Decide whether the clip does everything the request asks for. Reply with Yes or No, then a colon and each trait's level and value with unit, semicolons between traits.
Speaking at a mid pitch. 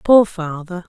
Yes: medium, 180 Hz